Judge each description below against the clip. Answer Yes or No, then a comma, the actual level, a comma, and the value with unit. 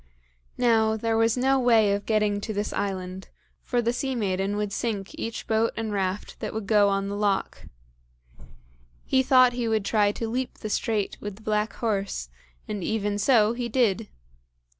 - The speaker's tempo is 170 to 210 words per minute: Yes, average, 180 wpm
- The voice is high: Yes, high, 215 Hz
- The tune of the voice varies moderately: No, narrow, 2.2 semitones